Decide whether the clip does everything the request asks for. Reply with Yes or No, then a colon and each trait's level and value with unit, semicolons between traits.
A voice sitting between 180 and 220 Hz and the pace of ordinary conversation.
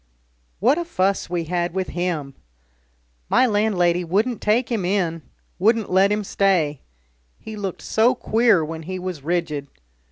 Yes: medium, 185 Hz; average, 150 wpm